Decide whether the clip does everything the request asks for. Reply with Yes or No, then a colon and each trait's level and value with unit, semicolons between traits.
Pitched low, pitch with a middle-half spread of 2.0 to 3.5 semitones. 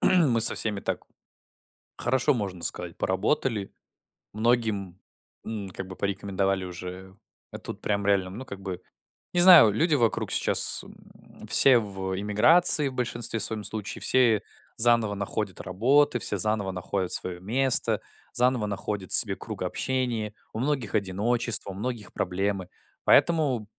No: low, 105 Hz; average, 4.1 semitones